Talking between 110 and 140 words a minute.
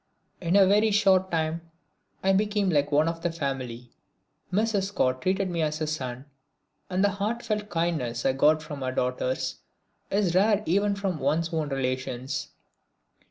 No: average, 160 wpm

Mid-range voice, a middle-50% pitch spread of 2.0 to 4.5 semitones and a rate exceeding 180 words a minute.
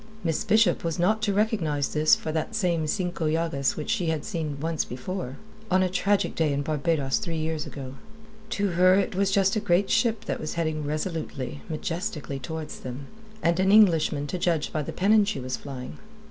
Yes: medium, 165 Hz; average, 4.2 semitones; average, 195 wpm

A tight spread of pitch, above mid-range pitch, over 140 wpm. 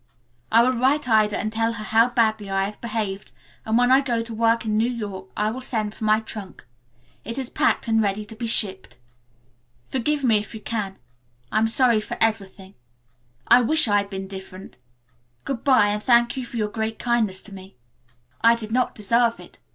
Yes: narrow, 2.3 semitones; high, 220 Hz; fast, 205 wpm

